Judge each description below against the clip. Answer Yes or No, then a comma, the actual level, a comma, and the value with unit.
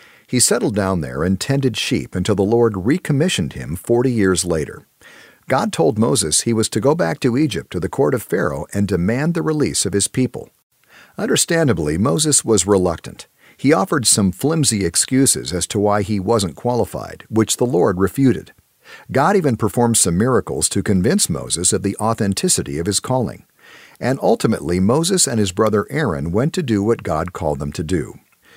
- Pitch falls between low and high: No, low, 105 Hz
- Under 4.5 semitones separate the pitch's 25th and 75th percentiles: No, average, 5.2 semitones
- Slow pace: No, average, 180 wpm